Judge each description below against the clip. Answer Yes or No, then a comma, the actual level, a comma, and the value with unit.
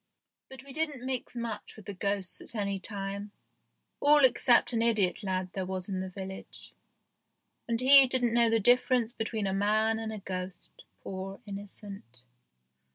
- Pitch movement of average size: Yes, average, 3.7 semitones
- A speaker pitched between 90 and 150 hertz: No, high, 210 Hz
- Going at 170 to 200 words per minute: No, average, 160 wpm